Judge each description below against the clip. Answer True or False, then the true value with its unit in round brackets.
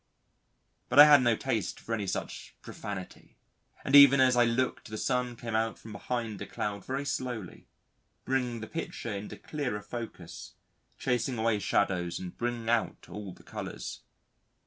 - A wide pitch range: False (3.4 semitones)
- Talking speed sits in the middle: True (160 wpm)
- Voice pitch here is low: True (115 Hz)